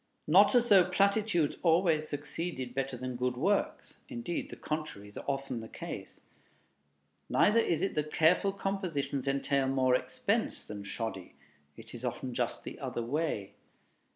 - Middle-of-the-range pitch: Yes, medium, 150 Hz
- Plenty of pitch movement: Yes, wide, 6.1 semitones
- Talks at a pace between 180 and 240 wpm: No, average, 150 wpm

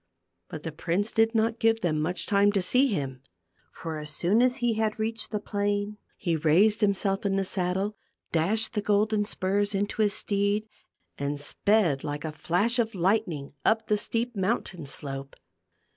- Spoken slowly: No, average, 175 wpm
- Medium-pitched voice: No, high, 200 Hz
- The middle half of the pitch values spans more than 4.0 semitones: Yes, average, 4.6 semitones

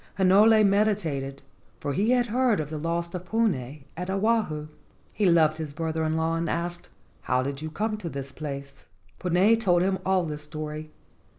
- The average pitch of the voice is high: No, medium, 170 Hz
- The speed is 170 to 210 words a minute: Yes, average, 180 wpm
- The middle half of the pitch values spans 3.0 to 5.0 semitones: Yes, average, 4.6 semitones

